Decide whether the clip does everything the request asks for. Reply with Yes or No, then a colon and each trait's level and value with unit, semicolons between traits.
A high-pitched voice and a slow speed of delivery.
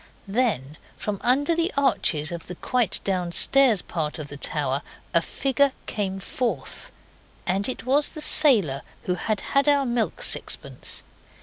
No: high, 210 Hz; average, 145 wpm